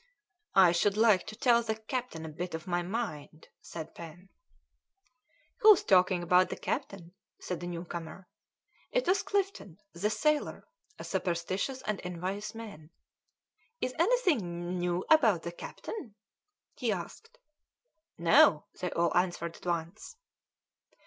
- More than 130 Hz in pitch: Yes, medium, 185 Hz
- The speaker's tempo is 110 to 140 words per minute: Yes, slow, 135 wpm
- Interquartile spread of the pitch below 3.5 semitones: No, average, 4.8 semitones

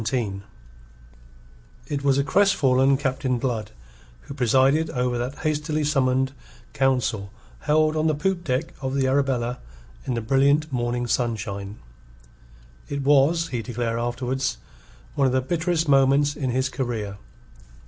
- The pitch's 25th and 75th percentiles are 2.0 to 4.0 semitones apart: Yes, average, 3.0 semitones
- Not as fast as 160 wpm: Yes, average, 140 wpm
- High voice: No, low, 135 Hz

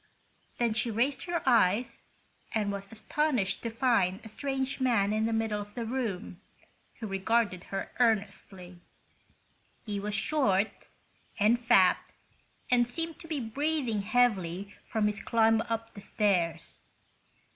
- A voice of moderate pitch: No, high, 220 Hz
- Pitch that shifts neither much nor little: Yes, average, 3.5 semitones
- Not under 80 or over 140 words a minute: Yes, slow, 135 wpm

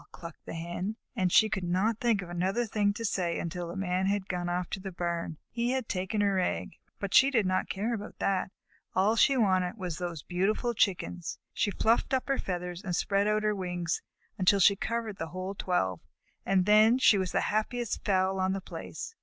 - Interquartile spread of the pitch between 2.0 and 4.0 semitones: Yes, average, 3.0 semitones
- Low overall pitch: No, high, 190 Hz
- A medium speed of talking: No, fast, 210 wpm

